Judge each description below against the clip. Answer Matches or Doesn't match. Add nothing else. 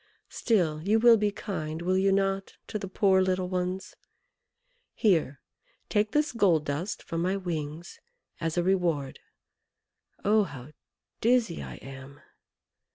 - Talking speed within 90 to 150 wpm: Matches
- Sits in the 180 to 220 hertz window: Matches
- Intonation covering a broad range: Doesn't match